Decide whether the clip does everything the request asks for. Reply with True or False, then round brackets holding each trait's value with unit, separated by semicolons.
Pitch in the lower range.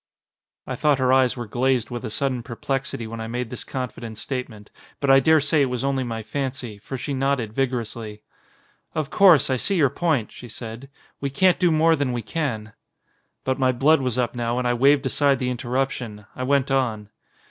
True (130 Hz)